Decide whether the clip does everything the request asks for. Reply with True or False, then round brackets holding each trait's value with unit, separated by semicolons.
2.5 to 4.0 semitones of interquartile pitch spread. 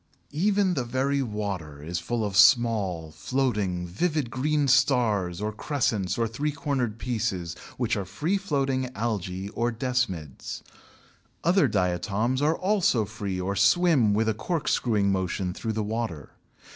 False (5.4 semitones)